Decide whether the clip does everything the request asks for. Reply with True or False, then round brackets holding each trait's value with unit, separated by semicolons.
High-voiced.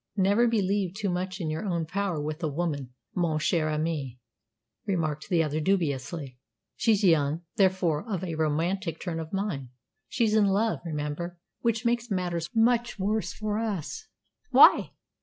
False (175 Hz)